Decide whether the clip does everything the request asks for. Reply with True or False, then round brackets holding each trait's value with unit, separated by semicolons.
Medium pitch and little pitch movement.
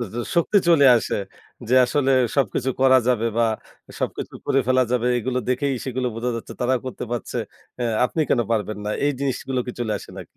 False (125 Hz; 2.0 semitones)